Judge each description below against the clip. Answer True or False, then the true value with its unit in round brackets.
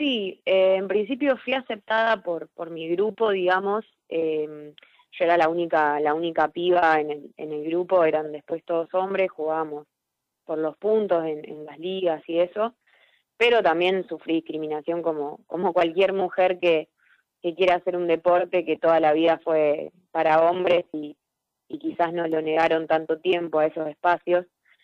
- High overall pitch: False (170 Hz)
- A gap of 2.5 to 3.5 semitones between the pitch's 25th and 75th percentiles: True (2.9 semitones)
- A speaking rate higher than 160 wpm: True (170 wpm)